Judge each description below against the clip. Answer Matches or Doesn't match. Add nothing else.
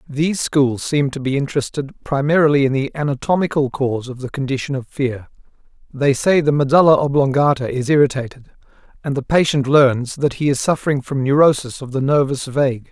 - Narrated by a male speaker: Matches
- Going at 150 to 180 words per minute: Matches